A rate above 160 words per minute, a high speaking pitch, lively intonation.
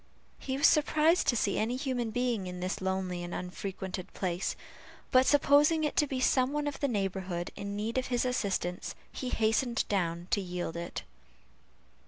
Yes: average, 175 wpm; high, 220 Hz; wide, 6.0 semitones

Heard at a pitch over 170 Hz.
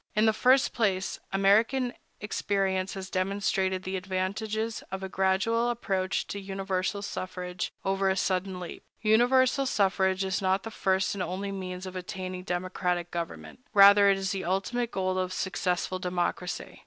Yes: high, 190 Hz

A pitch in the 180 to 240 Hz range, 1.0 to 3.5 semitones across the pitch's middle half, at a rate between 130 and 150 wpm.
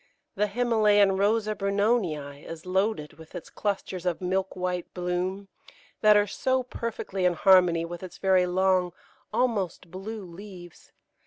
Yes: high, 190 Hz; average, 2.7 semitones; average, 140 wpm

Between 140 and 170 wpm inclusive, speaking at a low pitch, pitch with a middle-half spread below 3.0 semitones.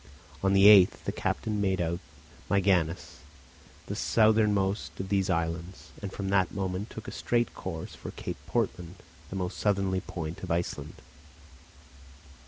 Yes: average, 145 wpm; very low, 95 Hz; narrow, 2.4 semitones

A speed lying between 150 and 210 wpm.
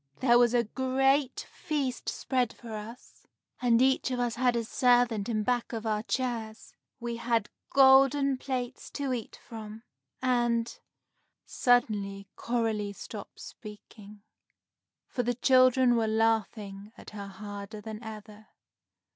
No: slow, 135 wpm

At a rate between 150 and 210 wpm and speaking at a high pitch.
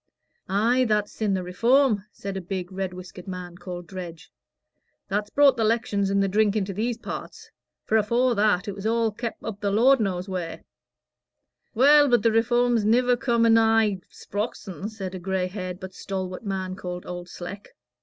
Yes: average, 175 wpm; high, 205 Hz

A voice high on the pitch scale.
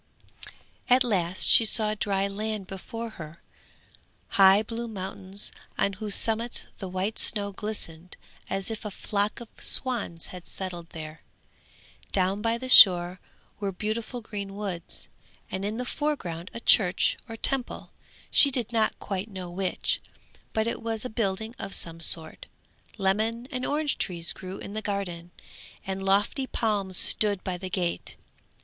Yes: high, 200 Hz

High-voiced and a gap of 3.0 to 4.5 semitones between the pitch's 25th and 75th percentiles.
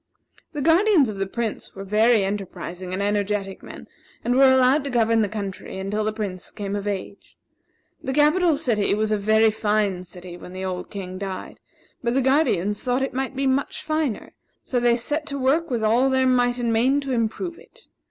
No: high, 225 Hz; average, 4.9 semitones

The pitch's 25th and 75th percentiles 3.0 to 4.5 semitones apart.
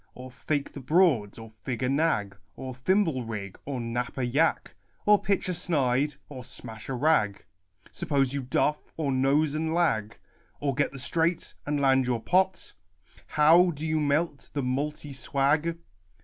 Yes: average, 3.9 semitones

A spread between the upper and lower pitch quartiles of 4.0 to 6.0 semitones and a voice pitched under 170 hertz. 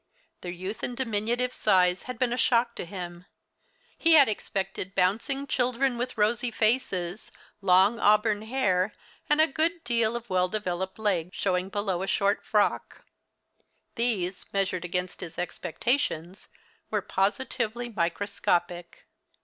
No: average, 4.7 semitones; high, 205 Hz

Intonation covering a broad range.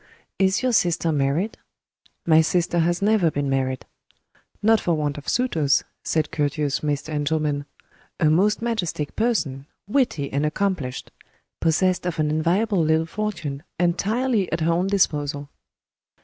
No: average, 4.8 semitones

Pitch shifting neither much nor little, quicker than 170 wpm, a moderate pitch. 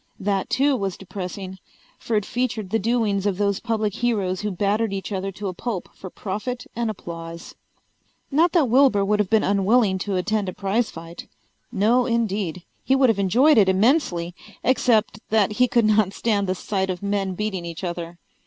No: average, 3.3 semitones; average, 185 wpm; high, 205 Hz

